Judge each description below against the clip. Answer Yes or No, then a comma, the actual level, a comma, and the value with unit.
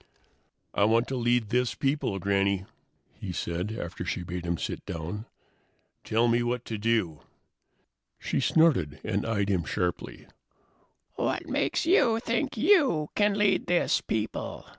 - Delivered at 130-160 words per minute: Yes, average, 145 wpm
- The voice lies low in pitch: Yes, low, 110 Hz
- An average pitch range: No, wide, 8.0 semitones